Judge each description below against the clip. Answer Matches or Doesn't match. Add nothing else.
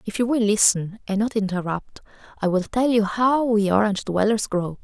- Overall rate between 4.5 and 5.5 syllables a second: Matches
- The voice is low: Doesn't match